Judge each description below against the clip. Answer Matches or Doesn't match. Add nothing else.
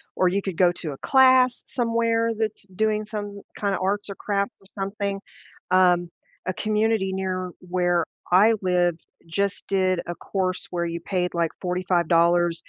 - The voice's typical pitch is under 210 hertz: Matches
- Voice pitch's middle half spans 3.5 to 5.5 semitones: Doesn't match